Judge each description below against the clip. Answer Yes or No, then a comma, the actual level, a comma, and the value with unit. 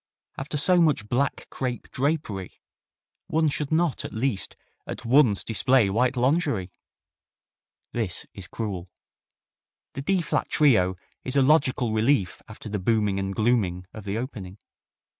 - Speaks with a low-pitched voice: Yes, low, 120 Hz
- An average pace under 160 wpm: Yes, average, 140 wpm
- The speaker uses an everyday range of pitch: No, wide, 5.8 semitones